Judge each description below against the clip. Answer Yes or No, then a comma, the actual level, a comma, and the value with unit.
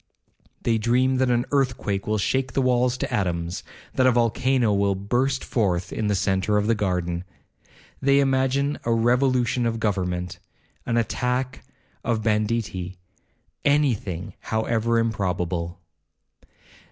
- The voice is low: Yes, low, 115 Hz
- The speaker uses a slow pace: Yes, slow, 125 wpm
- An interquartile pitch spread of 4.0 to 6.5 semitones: Yes, average, 4.7 semitones